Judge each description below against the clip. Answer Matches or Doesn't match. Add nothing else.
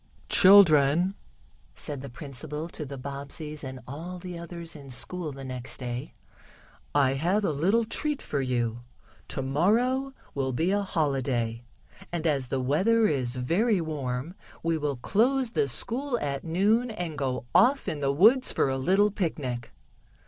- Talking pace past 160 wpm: Doesn't match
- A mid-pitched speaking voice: Matches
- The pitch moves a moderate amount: Doesn't match